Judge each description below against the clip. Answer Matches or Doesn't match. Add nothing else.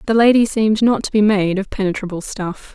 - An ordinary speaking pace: Doesn't match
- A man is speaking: Doesn't match